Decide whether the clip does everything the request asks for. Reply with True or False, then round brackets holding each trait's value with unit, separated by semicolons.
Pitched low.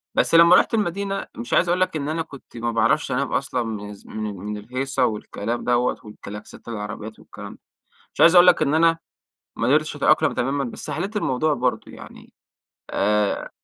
True (125 Hz)